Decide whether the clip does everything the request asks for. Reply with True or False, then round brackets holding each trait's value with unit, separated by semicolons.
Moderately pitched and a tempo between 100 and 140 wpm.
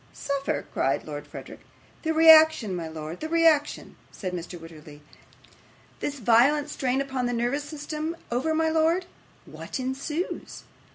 False (275 Hz; 135 wpm)